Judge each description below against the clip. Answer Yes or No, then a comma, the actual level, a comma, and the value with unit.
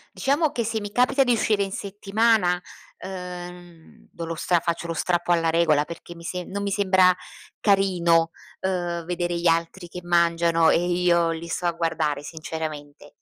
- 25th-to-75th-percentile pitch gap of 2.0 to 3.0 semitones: Yes, narrow, 2.4 semitones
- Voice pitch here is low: No, medium, 175 Hz